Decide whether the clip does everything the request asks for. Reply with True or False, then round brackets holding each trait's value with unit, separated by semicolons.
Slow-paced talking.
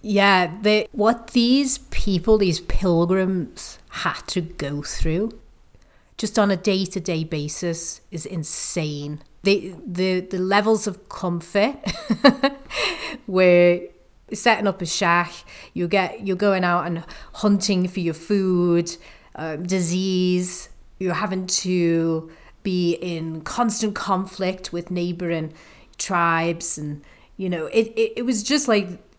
True (125 wpm)